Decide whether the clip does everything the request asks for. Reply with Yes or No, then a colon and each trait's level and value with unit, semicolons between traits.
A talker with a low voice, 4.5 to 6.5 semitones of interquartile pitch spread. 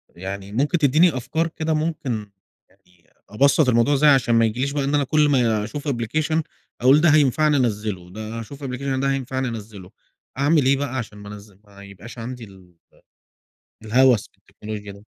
Yes: low, 125 Hz; average, 5.2 semitones